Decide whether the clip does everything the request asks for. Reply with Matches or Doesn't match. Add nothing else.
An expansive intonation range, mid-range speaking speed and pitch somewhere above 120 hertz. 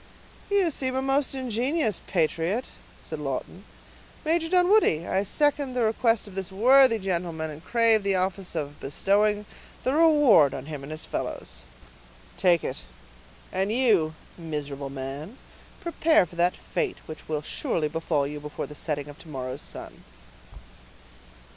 Matches